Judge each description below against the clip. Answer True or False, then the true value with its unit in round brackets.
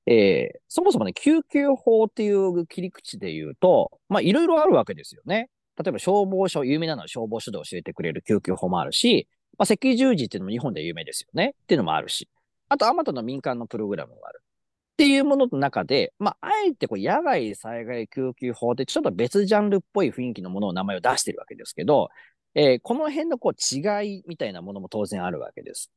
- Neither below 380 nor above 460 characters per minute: True (440 characters per minute)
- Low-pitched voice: False (195 Hz)